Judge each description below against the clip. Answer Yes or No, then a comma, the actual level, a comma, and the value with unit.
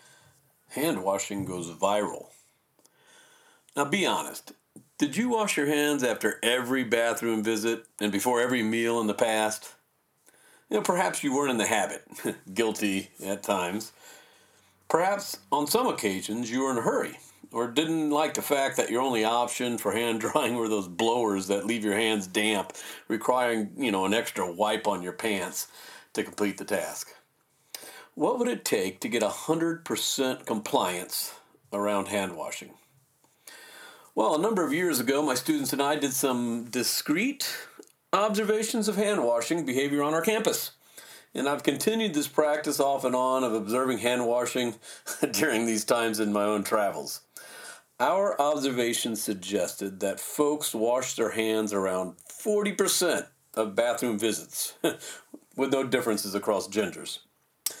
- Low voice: Yes, low, 120 Hz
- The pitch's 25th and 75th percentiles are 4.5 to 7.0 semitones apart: Yes, wide, 5.5 semitones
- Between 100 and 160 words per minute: Yes, average, 150 wpm